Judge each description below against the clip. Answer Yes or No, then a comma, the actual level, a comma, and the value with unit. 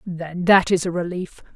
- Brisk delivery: No, average, 195 wpm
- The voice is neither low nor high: Yes, medium, 175 Hz